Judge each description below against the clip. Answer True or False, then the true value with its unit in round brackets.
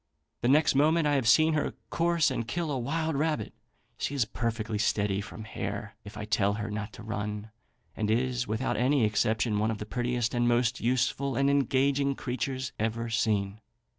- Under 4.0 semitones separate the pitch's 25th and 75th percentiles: False (4.3 semitones)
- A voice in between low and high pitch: False (120 Hz)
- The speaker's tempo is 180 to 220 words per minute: True (185 wpm)